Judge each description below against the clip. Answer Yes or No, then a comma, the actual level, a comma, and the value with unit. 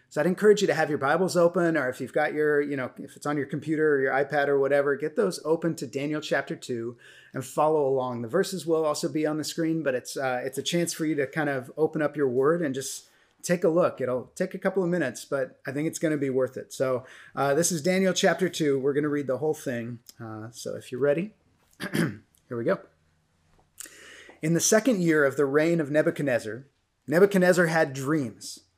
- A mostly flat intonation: No, average, 3.9 semitones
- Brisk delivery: Yes, fast, 235 wpm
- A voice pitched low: No, medium, 150 Hz